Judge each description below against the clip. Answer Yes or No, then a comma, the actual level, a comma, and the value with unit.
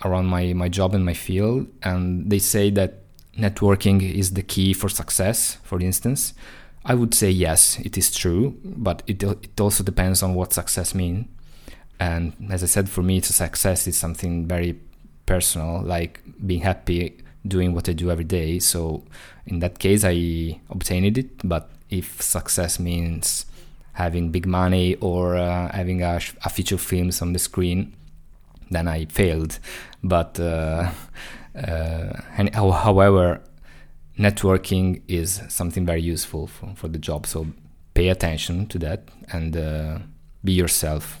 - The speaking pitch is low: Yes, very low, 90 Hz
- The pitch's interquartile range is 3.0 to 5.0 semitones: No, narrow, 2.5 semitones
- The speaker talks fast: No, average, 155 wpm